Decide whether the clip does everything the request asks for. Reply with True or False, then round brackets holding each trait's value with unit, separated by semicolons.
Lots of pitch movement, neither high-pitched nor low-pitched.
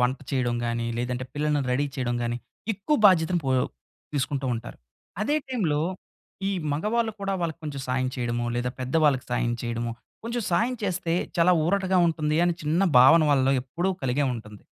True (5.8 semitones; 145 Hz)